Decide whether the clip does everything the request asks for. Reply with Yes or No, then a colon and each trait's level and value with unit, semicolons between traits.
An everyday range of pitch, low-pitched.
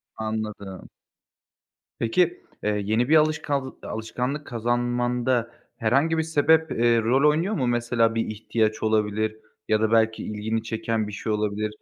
Yes: average, 3.4 semitones; low, 115 Hz